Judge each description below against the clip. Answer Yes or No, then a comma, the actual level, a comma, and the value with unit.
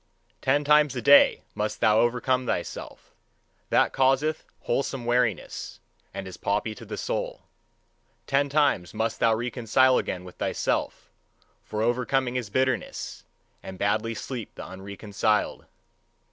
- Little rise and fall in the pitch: No, average, 3.7 semitones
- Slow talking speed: Yes, slow, 130 wpm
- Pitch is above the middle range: No, low, 120 Hz